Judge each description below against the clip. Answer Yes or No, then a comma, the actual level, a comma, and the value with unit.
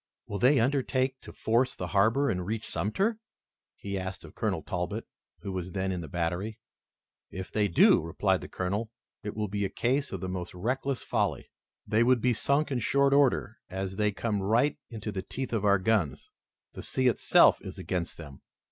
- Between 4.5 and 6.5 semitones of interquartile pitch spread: Yes, average, 4.9 semitones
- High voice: No, low, 105 Hz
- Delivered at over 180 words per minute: Yes, average, 190 wpm